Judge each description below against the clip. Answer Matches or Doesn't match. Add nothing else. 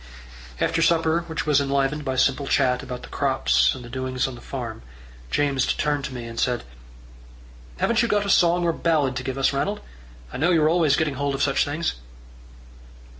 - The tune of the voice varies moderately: Matches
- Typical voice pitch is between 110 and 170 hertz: Matches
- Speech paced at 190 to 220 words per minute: Matches